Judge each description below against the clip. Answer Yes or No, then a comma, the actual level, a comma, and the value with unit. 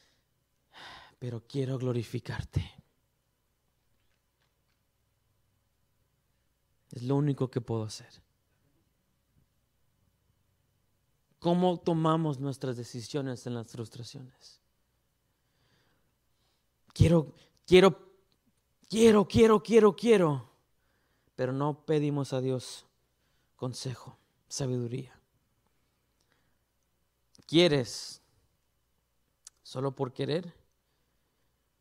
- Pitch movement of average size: Yes, average, 4.7 semitones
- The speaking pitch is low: Yes, low, 130 Hz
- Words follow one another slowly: Yes, slow, 60 wpm